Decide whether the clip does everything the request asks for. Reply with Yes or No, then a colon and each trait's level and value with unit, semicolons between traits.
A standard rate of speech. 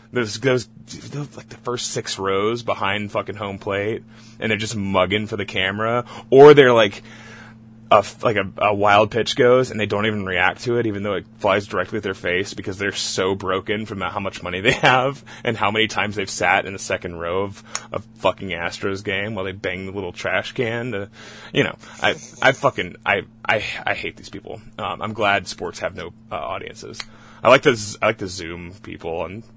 No: fast, 215 wpm